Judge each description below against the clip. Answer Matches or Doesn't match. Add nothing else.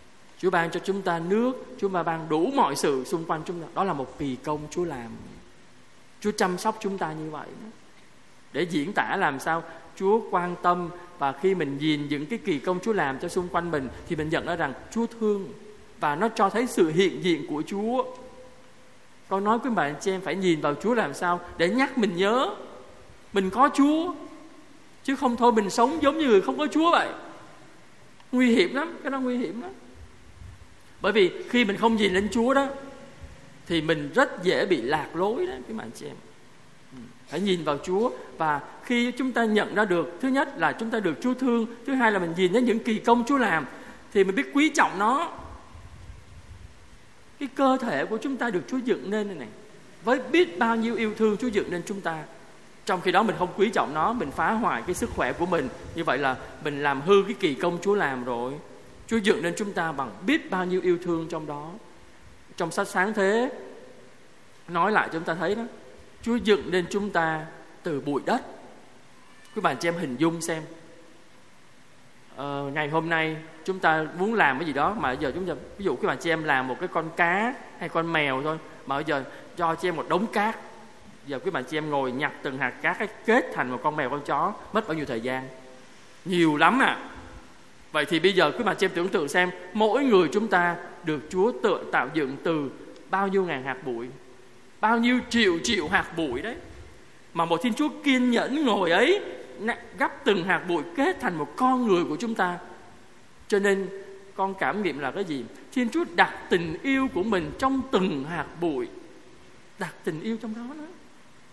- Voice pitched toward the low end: Doesn't match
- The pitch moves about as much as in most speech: Doesn't match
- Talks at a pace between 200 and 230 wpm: Matches